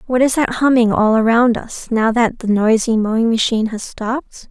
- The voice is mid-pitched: No, high, 230 Hz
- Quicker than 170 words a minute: Yes, average, 200 wpm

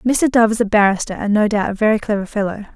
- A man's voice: No, female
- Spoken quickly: Yes, fast, 260 wpm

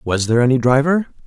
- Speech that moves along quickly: No, average, 190 wpm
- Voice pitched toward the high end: No, low, 135 Hz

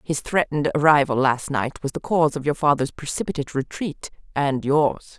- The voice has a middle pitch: Yes, medium, 145 Hz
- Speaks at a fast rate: No, average, 175 wpm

